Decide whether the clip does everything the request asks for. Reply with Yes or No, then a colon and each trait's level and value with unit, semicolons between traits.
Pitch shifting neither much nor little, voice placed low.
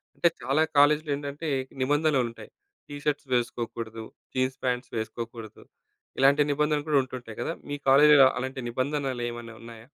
Yes: average, 3.7 semitones; low, 130 Hz